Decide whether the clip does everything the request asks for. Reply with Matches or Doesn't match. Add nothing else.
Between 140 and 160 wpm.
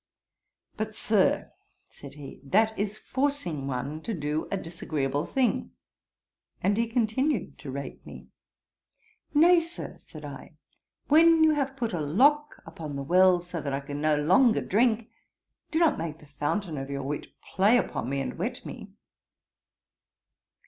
Matches